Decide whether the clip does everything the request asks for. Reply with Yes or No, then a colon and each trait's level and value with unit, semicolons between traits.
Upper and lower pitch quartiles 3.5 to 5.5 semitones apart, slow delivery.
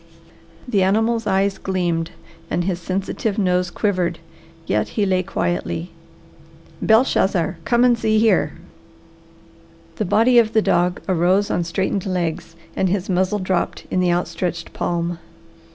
No: average, 3.1 semitones; slow, 130 wpm